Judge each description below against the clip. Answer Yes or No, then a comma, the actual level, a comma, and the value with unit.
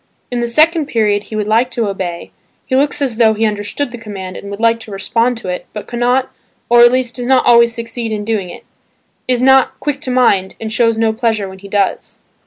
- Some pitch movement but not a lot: Yes, average, 3.0 semitones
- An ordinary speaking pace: No, fast, 225 wpm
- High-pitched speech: Yes, high, 230 Hz